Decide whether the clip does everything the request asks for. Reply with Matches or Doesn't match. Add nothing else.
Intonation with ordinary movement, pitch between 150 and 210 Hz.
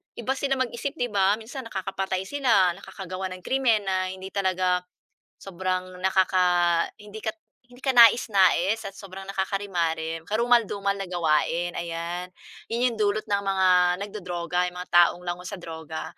Matches